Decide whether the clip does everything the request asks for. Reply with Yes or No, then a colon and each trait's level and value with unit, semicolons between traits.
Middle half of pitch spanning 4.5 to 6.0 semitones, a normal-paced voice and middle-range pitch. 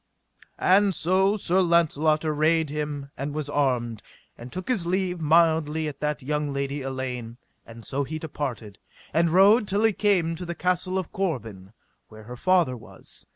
Yes: average, 4.9 semitones; average, 165 wpm; medium, 155 Hz